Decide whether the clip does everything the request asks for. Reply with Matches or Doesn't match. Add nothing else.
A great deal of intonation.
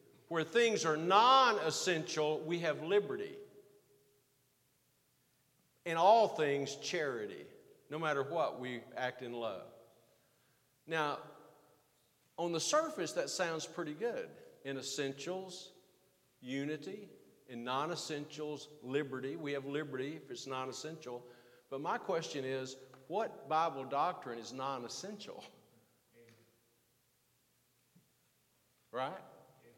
Doesn't match